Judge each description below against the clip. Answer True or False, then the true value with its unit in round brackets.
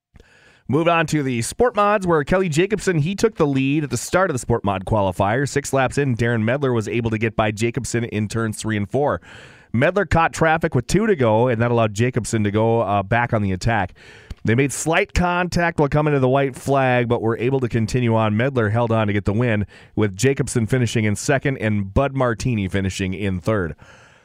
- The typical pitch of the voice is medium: False (120 Hz)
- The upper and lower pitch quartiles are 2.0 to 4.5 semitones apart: True (4.2 semitones)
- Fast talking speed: True (220 wpm)